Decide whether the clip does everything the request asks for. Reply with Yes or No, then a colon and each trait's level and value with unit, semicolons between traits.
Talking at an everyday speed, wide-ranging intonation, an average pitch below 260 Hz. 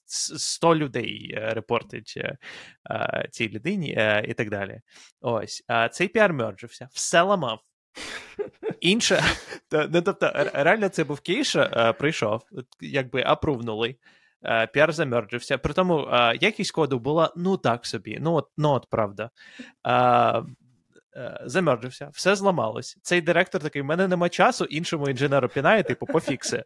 Yes: average, 130 wpm; wide, 6.6 semitones; medium, 140 Hz